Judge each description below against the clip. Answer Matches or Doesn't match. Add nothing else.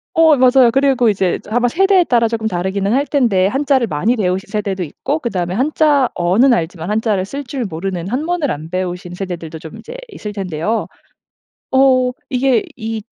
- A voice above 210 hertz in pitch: Matches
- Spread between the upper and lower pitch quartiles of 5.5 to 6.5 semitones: Matches